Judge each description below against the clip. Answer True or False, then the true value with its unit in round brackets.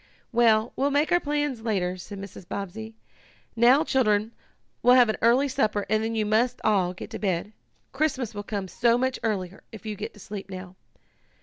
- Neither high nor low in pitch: False (220 Hz)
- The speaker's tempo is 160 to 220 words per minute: True (190 wpm)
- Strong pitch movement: False (3.6 semitones)